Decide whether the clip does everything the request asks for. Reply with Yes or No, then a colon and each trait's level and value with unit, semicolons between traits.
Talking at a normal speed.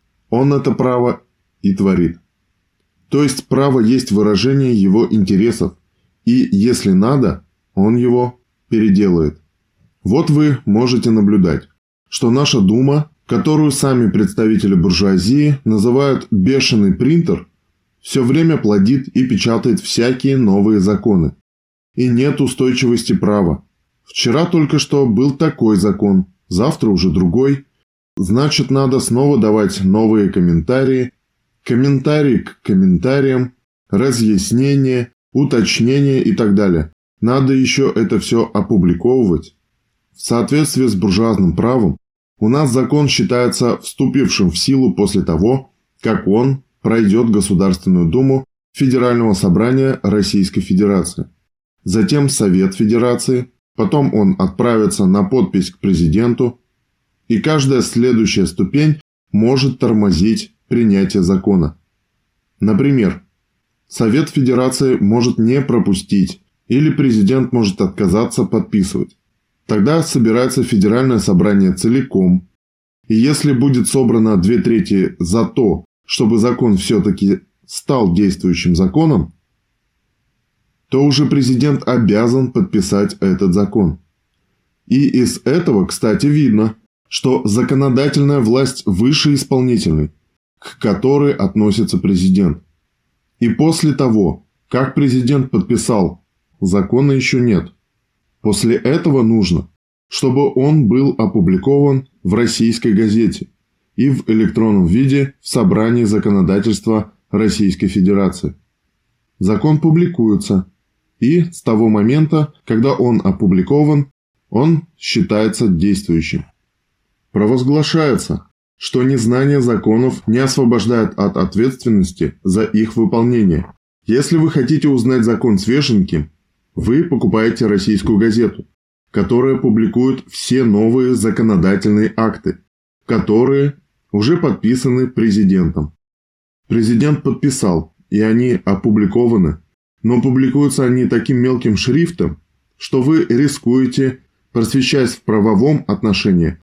No: slow, 105 wpm